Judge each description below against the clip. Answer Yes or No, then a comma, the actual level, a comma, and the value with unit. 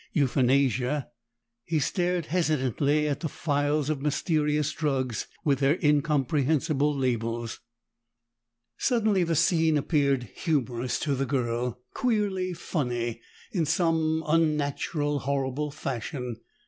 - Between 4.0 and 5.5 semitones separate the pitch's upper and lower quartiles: No, average, 3.3 semitones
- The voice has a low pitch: No, medium, 145 Hz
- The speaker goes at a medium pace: No, slow, 105 wpm